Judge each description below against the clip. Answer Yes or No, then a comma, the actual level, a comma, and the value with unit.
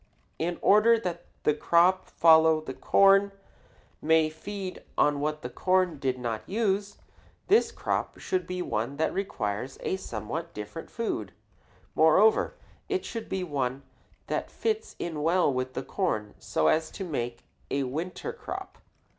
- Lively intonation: Yes, wide, 6.1 semitones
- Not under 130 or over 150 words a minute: Yes, average, 145 wpm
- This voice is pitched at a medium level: Yes, medium, 165 Hz